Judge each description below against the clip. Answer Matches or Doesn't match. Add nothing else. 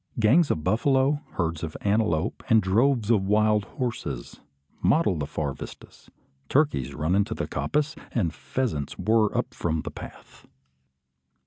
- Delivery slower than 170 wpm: Matches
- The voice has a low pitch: Matches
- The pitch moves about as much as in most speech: Doesn't match